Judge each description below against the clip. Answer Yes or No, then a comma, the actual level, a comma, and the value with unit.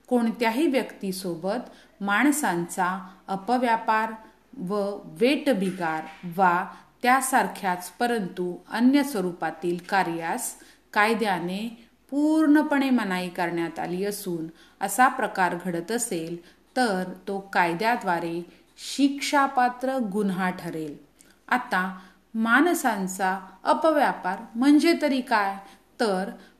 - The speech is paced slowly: Yes, slow, 80 wpm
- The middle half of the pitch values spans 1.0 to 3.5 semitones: No, wide, 5.5 semitones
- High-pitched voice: Yes, high, 200 Hz